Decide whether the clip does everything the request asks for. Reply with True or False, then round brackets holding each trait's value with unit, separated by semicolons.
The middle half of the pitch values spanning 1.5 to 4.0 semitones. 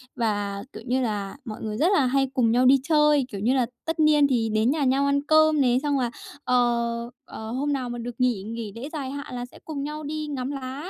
True (3.6 semitones)